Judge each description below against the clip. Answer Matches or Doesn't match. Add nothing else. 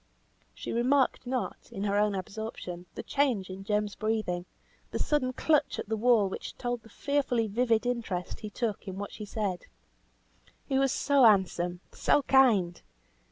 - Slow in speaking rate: Doesn't match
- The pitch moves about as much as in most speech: Matches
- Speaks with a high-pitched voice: Matches